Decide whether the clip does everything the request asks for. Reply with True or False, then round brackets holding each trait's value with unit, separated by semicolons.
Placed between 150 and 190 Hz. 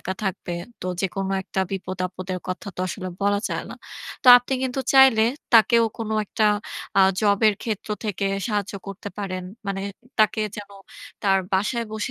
False (200 Hz)